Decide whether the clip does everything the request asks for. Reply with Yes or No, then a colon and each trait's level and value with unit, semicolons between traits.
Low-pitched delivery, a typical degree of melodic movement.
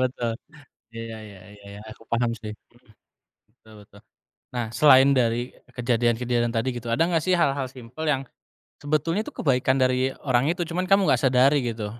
Yes: low, 125 Hz; average, 3.2 semitones